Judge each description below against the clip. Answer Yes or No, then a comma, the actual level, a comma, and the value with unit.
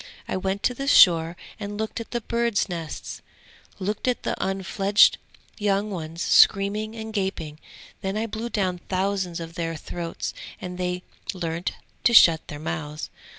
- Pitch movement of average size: Yes, average, 3.9 semitones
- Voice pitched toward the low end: No, high, 190 Hz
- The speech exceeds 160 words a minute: No, average, 155 wpm